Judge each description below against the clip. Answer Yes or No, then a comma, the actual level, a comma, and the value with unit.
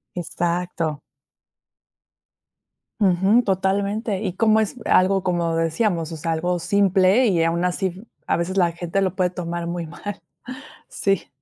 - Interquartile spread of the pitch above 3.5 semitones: No, narrow, 2.4 semitones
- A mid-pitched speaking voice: Yes, medium, 180 Hz